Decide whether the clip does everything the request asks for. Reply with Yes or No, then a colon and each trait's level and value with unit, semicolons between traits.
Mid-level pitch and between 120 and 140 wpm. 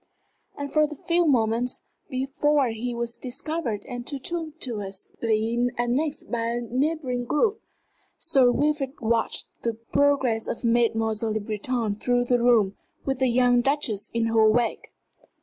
No: high, 245 Hz; slow, 135 wpm